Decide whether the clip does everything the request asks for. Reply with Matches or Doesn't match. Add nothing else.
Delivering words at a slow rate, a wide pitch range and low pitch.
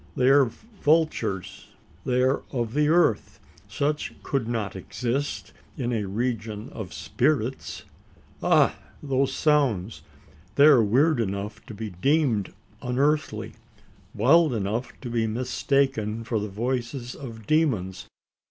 Doesn't match